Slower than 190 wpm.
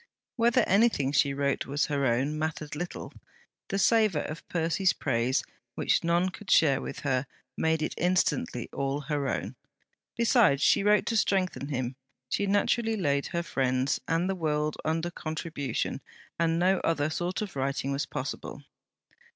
Yes: average, 155 wpm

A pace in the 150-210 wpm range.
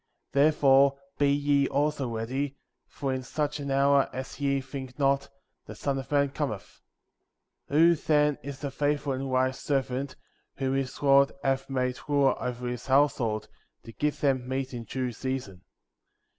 Yes: average, 165 wpm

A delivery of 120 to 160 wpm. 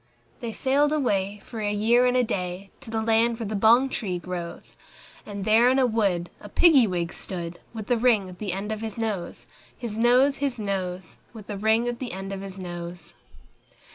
No: fast, 205 wpm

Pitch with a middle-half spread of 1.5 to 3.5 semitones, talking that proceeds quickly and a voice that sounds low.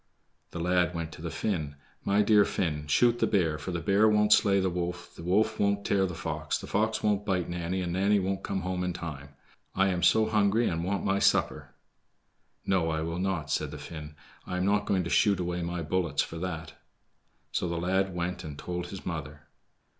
Yes: average, 3.0 semitones; fast, 215 wpm; very low, 90 Hz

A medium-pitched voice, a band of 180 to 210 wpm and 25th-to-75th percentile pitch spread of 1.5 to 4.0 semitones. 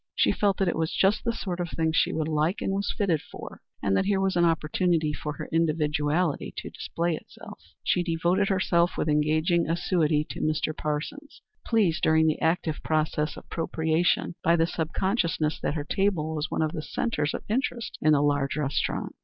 Yes: medium, 165 Hz; average, 195 wpm; average, 2.9 semitones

